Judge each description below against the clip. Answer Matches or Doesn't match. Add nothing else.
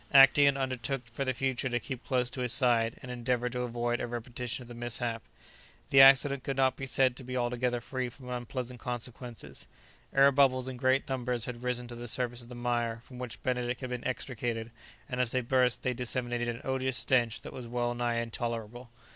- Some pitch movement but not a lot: Doesn't match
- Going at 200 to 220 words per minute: Matches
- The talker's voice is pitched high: Doesn't match